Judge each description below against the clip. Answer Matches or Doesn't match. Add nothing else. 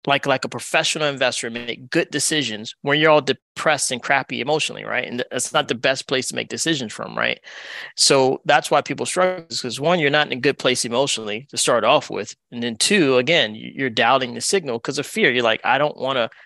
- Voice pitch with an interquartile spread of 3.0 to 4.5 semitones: Matches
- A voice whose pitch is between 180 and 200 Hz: Doesn't match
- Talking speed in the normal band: Doesn't match